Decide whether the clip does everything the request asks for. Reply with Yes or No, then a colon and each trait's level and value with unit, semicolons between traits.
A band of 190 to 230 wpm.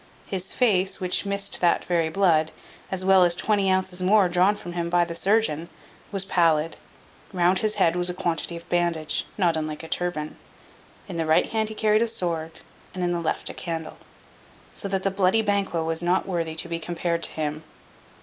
Yes: average, 200 wpm